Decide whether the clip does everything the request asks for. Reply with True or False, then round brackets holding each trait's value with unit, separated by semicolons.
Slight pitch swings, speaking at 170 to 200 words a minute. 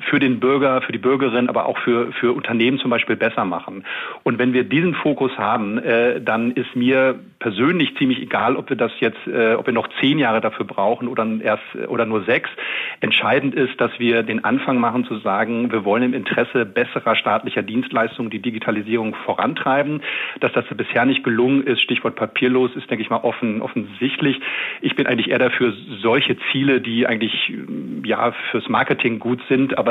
True (2.3 semitones; 185 wpm)